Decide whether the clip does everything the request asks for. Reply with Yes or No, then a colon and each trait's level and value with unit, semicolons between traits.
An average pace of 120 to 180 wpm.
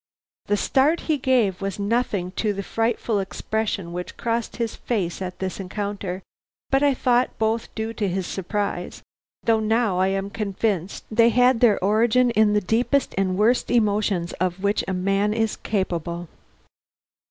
Yes: average, 160 wpm